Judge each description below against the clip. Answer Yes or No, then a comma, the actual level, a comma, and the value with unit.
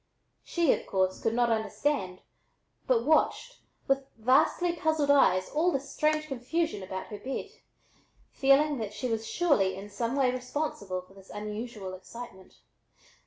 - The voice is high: Yes, high, 245 Hz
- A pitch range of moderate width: No, wide, 6.3 semitones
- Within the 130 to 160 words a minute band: Yes, average, 145 wpm